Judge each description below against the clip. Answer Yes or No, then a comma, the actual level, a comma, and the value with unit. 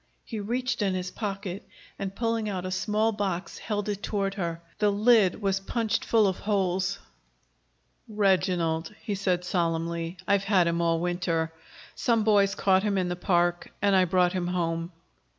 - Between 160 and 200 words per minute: Yes, average, 170 wpm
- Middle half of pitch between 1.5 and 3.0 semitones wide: Yes, average, 2.7 semitones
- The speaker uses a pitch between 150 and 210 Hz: Yes, high, 190 Hz